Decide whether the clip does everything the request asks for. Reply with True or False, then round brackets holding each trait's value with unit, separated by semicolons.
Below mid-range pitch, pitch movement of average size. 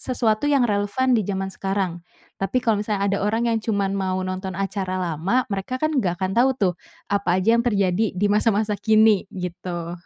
False (200 Hz; 3.0 semitones)